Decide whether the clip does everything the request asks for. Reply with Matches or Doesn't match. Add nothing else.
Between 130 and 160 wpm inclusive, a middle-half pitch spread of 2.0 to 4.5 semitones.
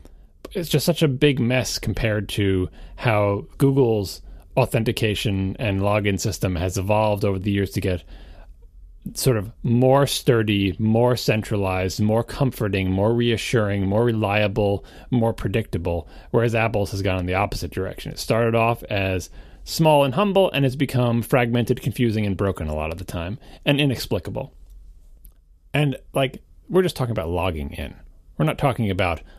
Doesn't match